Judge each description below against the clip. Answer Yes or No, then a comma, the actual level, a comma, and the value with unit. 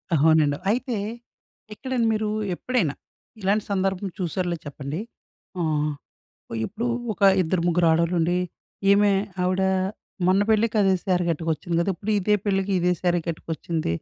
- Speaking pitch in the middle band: Yes, medium, 180 Hz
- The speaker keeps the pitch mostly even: No, average, 3.7 semitones